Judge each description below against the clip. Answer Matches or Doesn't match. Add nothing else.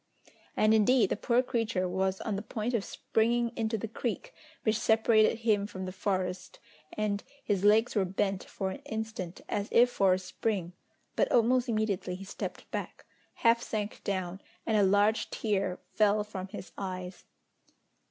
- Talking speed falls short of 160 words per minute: Doesn't match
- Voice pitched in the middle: Doesn't match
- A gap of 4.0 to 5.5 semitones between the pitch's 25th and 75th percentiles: Doesn't match